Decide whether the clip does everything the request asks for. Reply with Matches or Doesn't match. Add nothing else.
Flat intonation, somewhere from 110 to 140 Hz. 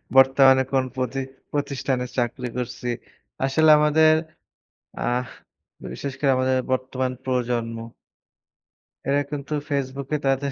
Matches